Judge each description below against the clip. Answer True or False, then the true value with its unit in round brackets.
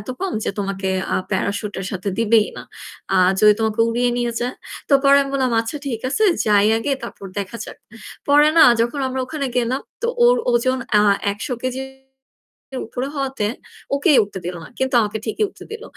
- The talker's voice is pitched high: True (240 Hz)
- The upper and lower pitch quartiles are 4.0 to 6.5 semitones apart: True (4.6 semitones)